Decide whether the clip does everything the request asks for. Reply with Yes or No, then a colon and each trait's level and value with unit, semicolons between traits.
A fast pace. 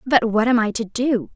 Yes: fast, 265 wpm